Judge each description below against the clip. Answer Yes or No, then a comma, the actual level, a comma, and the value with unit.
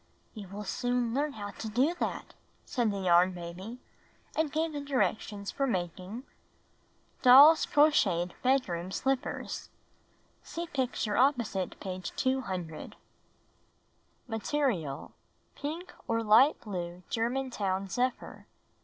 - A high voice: Yes, high, 230 Hz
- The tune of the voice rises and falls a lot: Yes, wide, 6.2 semitones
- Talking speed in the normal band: No, slow, 115 wpm